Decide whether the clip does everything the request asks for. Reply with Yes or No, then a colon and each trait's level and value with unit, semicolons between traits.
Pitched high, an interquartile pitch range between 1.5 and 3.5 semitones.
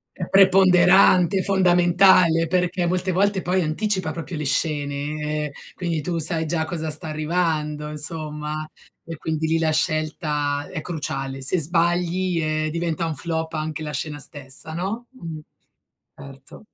No: medium, 160 Hz; average, 2.7 semitones